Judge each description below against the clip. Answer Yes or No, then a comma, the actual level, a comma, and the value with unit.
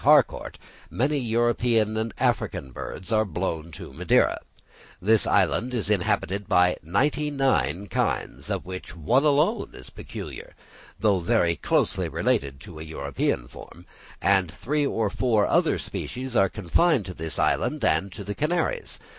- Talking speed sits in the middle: Yes, average, 145 wpm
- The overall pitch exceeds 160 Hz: No, low, 105 Hz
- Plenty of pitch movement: Yes, wide, 6.2 semitones